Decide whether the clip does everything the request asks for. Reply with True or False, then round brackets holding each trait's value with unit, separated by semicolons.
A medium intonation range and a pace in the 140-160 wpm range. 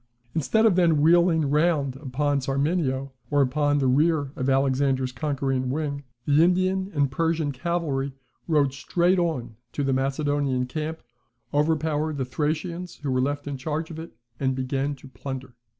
True (3.1 semitones; 155 wpm)